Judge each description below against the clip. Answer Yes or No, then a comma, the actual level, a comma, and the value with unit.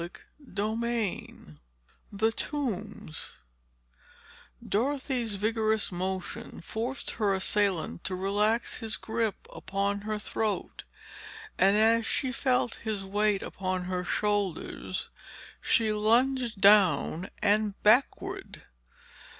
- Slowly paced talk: Yes, slow, 95 wpm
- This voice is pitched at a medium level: No, high, 210 Hz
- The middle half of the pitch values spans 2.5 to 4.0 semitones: Yes, average, 2.9 semitones